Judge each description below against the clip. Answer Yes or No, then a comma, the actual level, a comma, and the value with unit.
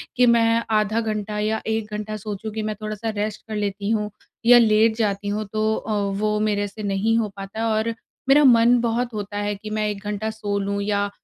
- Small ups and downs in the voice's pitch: Yes, narrow, 1.4 semitones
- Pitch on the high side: Yes, high, 215 Hz